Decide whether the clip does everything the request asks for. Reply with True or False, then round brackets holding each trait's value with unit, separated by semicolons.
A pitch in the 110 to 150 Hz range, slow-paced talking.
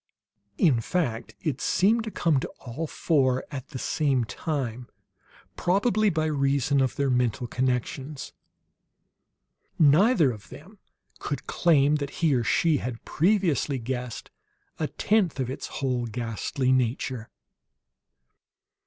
True (140 Hz; 125 wpm)